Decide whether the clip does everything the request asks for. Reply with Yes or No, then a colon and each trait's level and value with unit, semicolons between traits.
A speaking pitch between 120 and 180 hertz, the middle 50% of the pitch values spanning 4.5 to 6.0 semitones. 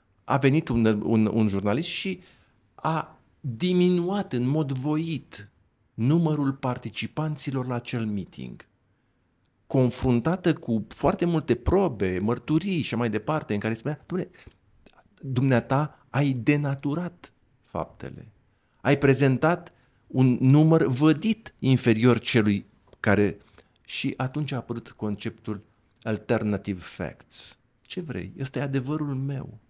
Yes: low, 125 Hz; average, 5.2 semitones